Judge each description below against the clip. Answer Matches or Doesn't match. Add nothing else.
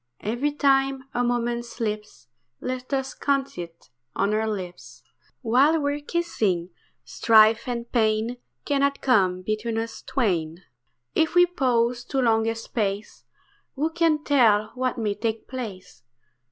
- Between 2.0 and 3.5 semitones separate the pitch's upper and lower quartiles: Doesn't match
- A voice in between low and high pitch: Doesn't match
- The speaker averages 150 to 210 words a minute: Doesn't match